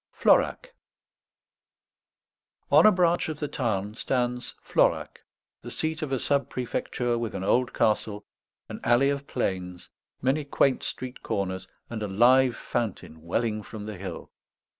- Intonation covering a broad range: No, average, 4.7 semitones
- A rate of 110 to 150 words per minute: Yes, average, 140 wpm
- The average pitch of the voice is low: Yes, low, 120 Hz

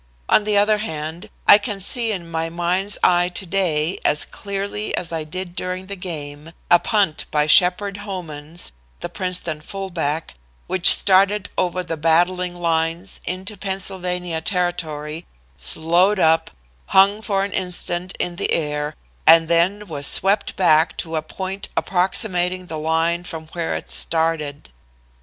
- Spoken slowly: No, average, 145 wpm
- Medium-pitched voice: Yes, medium, 175 Hz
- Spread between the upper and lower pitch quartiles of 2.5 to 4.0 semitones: Yes, average, 3.0 semitones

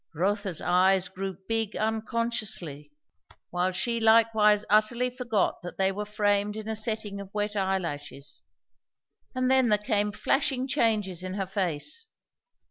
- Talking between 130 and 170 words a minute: Yes, slow, 135 wpm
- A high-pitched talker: Yes, high, 210 Hz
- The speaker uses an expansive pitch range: No, average, 2.9 semitones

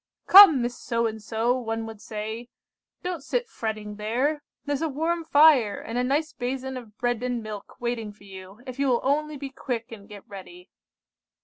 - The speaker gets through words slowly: No, average, 190 wpm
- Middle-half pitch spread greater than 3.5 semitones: Yes, average, 4.5 semitones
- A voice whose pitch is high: Yes, high, 245 Hz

